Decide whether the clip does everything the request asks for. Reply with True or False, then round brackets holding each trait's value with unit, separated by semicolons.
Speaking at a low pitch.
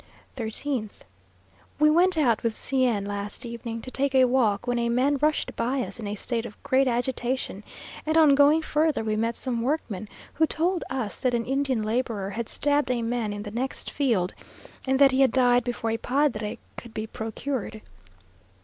False (245 Hz)